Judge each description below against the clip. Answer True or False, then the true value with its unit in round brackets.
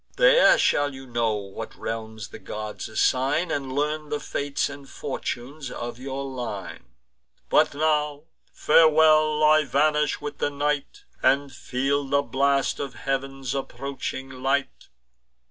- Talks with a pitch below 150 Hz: True (140 Hz)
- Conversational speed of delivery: False (130 wpm)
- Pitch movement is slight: True (2.3 semitones)